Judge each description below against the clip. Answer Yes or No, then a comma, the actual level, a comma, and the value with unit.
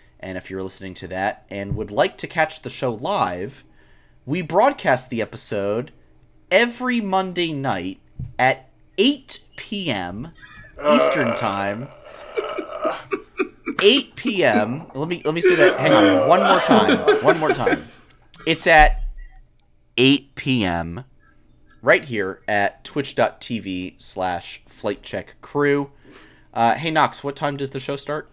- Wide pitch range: Yes, wide, 8.1 semitones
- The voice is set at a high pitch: No, medium, 140 Hz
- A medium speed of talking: No, slow, 125 wpm